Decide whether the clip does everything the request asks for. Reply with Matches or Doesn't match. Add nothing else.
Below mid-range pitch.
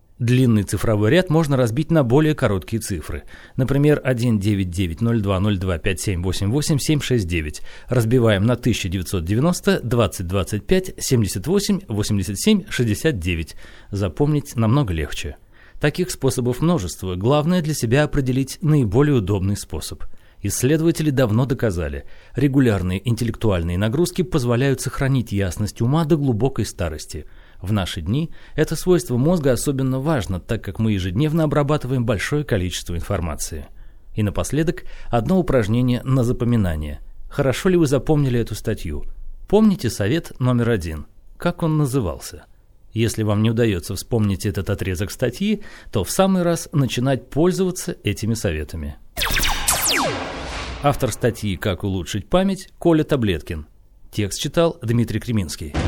Matches